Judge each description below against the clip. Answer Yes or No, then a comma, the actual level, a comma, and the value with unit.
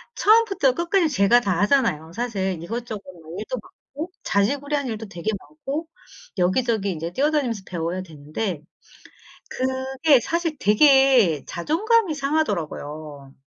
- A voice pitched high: Yes, high, 235 Hz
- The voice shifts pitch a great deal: Yes, wide, 8.4 semitones